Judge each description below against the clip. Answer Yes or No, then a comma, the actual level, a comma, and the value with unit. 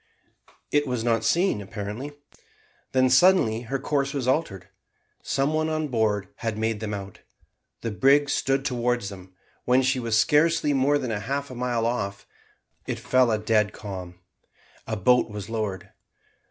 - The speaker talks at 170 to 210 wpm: No, average, 155 wpm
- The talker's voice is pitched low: Yes, low, 120 Hz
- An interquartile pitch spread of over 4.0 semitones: Yes, average, 4.4 semitones